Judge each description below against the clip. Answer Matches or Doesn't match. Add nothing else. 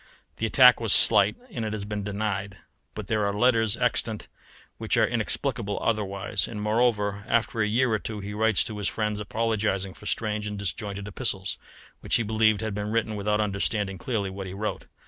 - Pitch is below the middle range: Matches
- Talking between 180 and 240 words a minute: Matches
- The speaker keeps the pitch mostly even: Matches